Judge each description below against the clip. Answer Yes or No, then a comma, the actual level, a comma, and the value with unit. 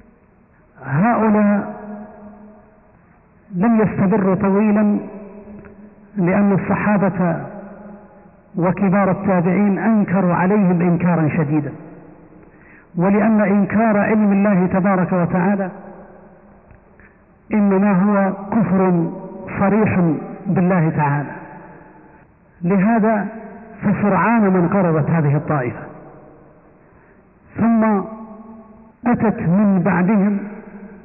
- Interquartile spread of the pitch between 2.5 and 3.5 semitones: Yes, average, 2.8 semitones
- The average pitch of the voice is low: No, high, 195 Hz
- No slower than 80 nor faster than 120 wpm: No, slow, 65 wpm